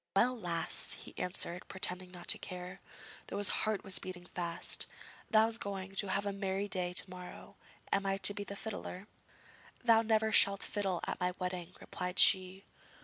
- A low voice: No, high, 190 Hz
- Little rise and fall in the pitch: Yes, narrow, 2.0 semitones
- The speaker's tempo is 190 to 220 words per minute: No, average, 175 wpm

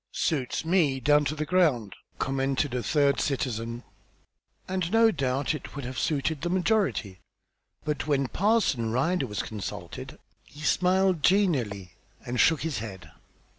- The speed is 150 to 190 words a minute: No, average, 140 wpm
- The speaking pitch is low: No, medium, 145 Hz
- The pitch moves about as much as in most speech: No, wide, 5.9 semitones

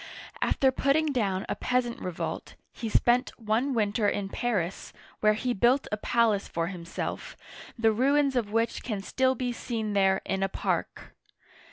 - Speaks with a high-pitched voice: Yes, high, 225 Hz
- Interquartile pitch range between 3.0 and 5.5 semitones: Yes, average, 3.7 semitones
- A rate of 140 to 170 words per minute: Yes, average, 165 wpm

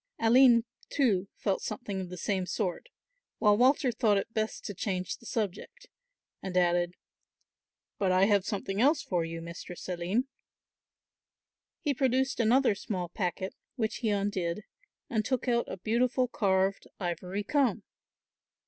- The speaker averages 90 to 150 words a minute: Yes, average, 140 wpm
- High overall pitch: Yes, high, 205 Hz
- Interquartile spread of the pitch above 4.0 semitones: Yes, average, 4.7 semitones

